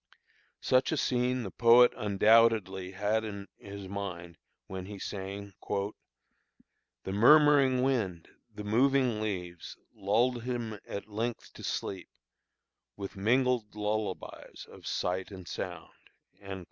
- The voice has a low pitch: Yes, low, 105 Hz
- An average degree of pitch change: Yes, average, 3.8 semitones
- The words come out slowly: Yes, slow, 115 wpm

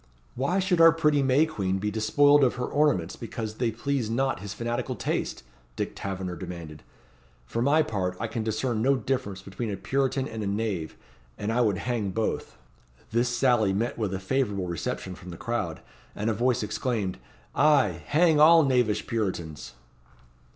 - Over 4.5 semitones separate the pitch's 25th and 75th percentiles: Yes, average, 5.3 semitones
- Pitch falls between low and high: No, low, 115 Hz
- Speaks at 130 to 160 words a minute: No, average, 170 wpm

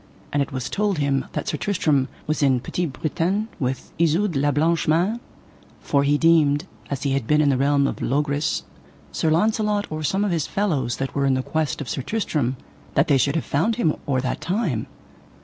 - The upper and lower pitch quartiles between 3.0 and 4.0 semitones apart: Yes, average, 3.6 semitones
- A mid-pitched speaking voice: Yes, medium, 150 Hz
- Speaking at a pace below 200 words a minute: No, fast, 205 wpm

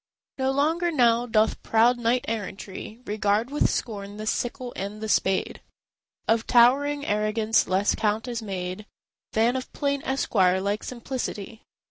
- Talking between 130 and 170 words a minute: Yes, average, 140 wpm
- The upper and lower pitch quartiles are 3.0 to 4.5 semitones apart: Yes, average, 3.3 semitones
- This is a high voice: Yes, high, 225 Hz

